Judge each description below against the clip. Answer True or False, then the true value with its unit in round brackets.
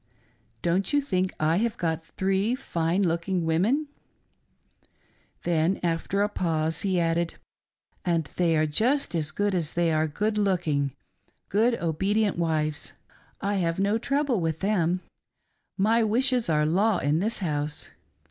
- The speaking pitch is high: False (180 Hz)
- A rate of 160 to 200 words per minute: False (150 wpm)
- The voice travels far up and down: False (4.3 semitones)